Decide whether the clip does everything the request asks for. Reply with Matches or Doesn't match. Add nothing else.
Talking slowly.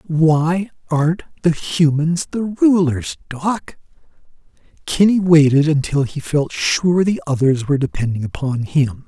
Matches